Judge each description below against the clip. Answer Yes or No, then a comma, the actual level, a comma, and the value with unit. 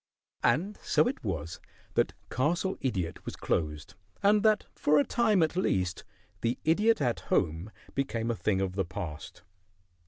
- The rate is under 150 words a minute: No, average, 155 wpm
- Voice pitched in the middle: No, low, 120 Hz